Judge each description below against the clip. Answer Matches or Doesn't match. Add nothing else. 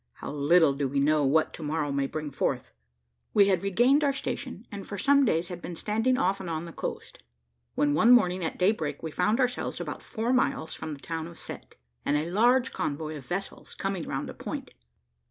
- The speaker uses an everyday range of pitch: Doesn't match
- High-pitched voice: Doesn't match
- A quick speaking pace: Matches